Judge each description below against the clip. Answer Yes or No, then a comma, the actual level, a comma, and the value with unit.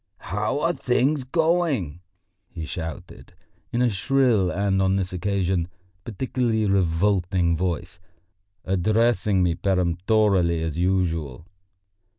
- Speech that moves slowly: Yes, slow, 105 wpm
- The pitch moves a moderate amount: Yes, average, 4.2 semitones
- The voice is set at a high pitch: No, very low, 95 Hz